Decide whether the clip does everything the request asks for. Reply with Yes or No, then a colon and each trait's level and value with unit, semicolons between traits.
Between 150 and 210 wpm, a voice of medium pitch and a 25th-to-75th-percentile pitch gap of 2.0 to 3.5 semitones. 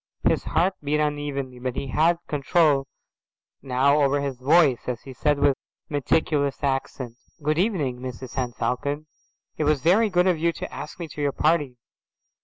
Yes: average, 170 wpm; medium, 145 Hz; average, 2.8 semitones